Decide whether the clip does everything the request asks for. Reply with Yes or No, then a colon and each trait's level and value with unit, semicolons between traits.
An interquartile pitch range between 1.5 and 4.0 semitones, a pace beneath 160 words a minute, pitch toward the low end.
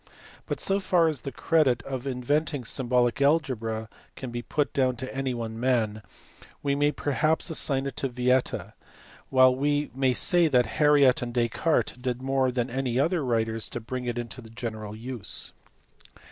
No: average, 2.9 semitones; average, 170 wpm; low, 130 Hz